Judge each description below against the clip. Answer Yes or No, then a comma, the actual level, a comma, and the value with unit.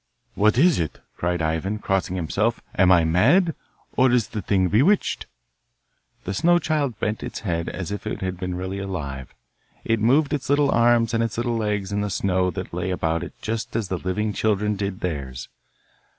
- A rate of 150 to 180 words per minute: No, average, 190 wpm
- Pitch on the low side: Yes, low, 100 Hz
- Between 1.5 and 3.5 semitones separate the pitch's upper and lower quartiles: No, average, 4.2 semitones